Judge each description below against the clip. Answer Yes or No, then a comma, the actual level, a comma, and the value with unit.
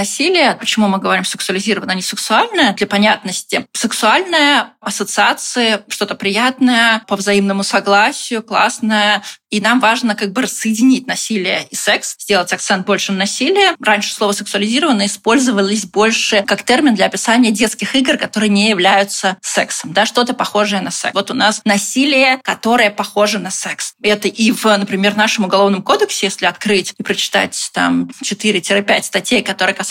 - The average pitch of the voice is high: Yes, high, 210 Hz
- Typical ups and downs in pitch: Yes, average, 3.0 semitones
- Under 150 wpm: No, average, 155 wpm